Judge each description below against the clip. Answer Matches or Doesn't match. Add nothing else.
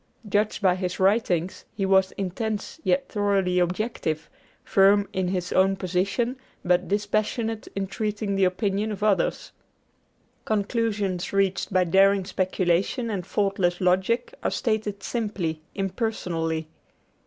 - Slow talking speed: Matches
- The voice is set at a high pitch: Matches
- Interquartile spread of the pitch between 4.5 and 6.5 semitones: Doesn't match